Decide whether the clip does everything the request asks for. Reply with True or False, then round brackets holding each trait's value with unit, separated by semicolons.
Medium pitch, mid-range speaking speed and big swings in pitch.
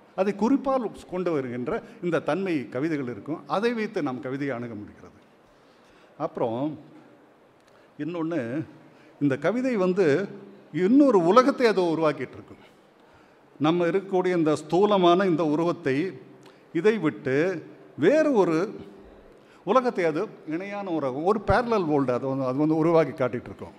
True (165 Hz; 115 wpm; 6.3 semitones)